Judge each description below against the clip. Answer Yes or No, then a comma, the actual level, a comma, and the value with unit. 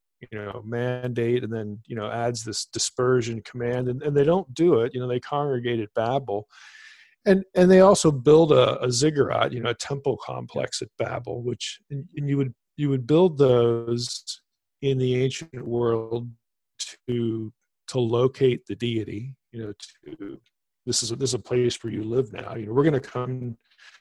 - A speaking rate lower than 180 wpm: No, average, 185 wpm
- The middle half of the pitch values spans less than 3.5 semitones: Yes, average, 2.9 semitones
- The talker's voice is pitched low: Yes, low, 125 Hz